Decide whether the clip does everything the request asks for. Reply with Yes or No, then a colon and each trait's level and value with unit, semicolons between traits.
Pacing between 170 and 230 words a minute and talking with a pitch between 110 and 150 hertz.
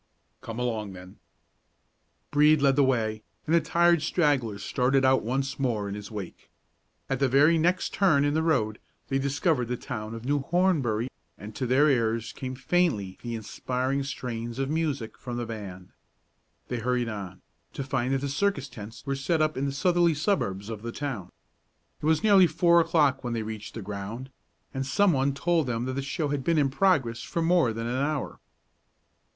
Yes: average, 190 wpm; low, 135 Hz